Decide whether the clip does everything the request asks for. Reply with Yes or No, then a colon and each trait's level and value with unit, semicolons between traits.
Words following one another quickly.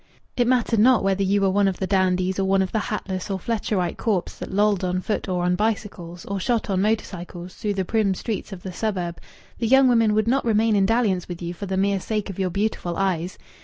Yes: fast, 240 wpm